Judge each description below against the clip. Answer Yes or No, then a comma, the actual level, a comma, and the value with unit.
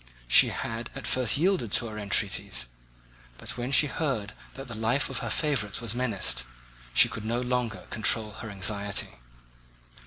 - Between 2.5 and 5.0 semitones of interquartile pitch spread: Yes, average, 3.3 semitones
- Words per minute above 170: No, average, 160 wpm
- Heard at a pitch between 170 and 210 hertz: No, low, 115 Hz